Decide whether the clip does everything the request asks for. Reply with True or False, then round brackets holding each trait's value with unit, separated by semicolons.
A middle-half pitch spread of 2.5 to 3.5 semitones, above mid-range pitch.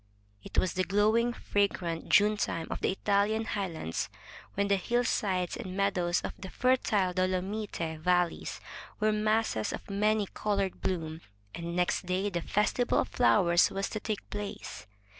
True (2.9 semitones; 195 Hz)